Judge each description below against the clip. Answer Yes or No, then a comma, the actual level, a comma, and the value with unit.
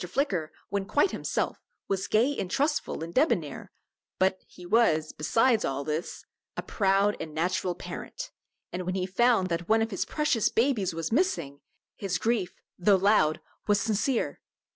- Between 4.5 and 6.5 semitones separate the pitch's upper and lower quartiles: Yes, average, 5.0 semitones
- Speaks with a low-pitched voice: No, high, 195 Hz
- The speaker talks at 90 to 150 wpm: No, average, 160 wpm